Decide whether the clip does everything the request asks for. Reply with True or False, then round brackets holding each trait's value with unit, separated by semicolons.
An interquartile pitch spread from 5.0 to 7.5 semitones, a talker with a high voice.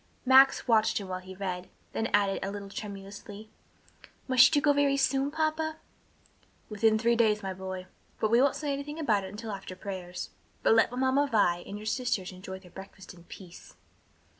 True (5.5 semitones; 210 Hz)